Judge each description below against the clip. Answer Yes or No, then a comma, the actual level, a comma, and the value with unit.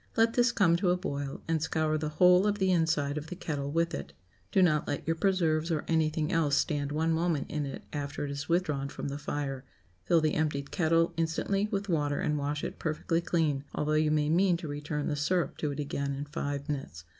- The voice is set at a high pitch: No, medium, 155 Hz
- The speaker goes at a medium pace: No, fast, 225 wpm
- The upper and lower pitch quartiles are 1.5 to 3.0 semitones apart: Yes, average, 2.7 semitones